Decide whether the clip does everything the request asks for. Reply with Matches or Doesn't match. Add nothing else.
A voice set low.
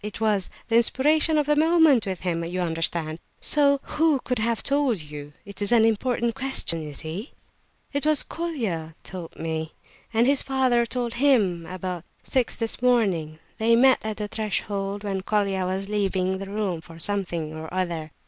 Doesn't match